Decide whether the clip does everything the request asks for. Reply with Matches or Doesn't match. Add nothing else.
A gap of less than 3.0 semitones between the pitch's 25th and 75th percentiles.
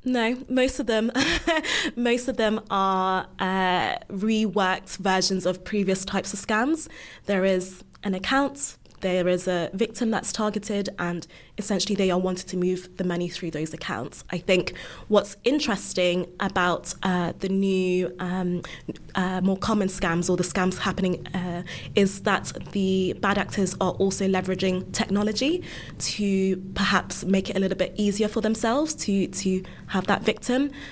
Matches